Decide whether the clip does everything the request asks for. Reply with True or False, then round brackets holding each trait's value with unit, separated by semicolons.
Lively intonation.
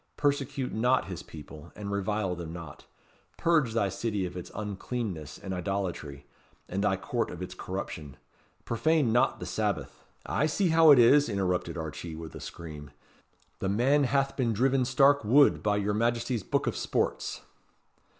True (6.1 semitones)